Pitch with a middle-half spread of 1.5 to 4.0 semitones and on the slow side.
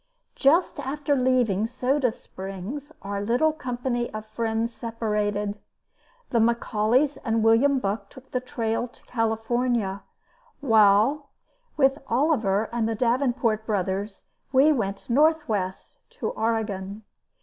Yes: average, 3.5 semitones; slow, 115 wpm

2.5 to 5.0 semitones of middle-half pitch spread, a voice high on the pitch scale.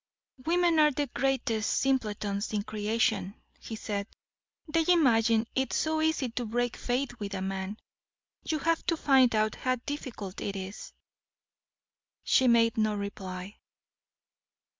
Yes: average, 4.6 semitones; high, 230 Hz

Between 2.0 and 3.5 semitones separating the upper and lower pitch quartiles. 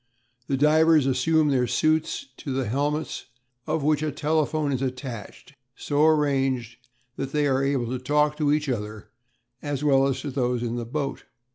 Yes: average, 2.8 semitones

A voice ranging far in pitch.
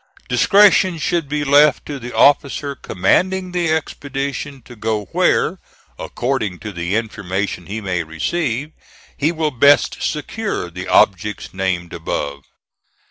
Yes: wide, 7.9 semitones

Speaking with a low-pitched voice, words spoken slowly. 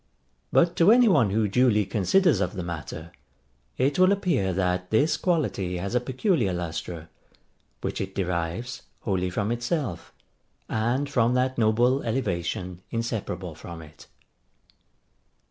Yes: low, 110 Hz; slow, 130 wpm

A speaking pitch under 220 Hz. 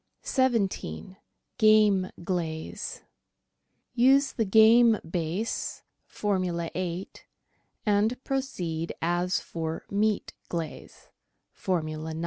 Yes: medium, 185 Hz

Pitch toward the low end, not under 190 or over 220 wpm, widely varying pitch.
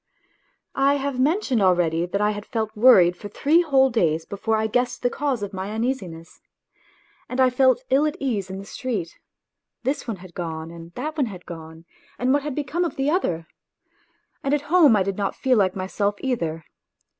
No: high, 220 Hz; average, 195 wpm; wide, 6.5 semitones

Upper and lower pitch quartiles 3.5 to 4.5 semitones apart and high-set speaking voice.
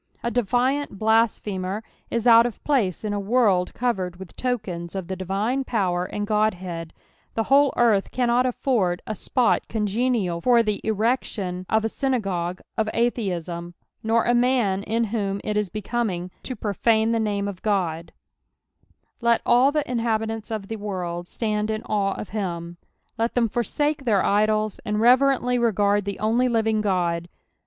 Yes: average, 3.8 semitones; high, 215 Hz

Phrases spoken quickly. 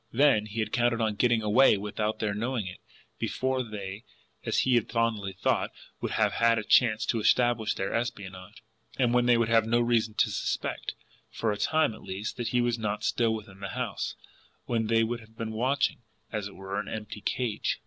Yes: fast, 210 wpm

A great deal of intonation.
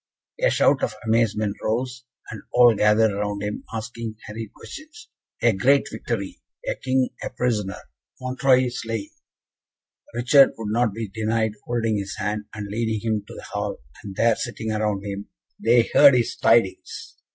No: narrow, 2.6 semitones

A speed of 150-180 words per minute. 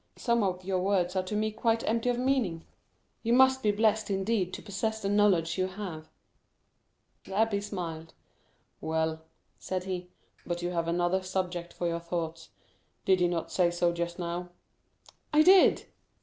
Yes: average, 165 wpm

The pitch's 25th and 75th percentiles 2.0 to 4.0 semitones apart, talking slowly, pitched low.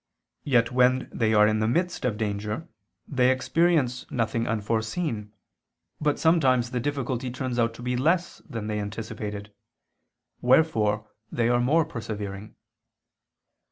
Yes: average, 3.4 semitones; slow, 130 wpm; low, 120 Hz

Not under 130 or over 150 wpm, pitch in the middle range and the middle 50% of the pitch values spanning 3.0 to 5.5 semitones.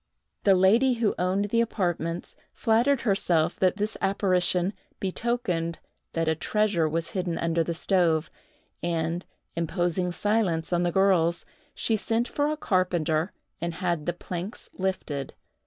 Yes: average, 140 wpm; medium, 180 Hz; average, 3.5 semitones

